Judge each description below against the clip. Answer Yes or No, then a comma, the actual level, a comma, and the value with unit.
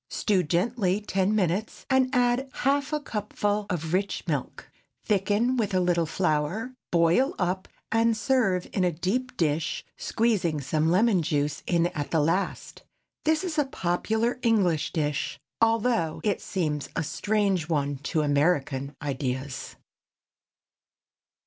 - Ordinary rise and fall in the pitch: No, wide, 6.1 semitones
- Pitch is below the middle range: No, medium, 185 Hz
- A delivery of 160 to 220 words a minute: No, slow, 135 wpm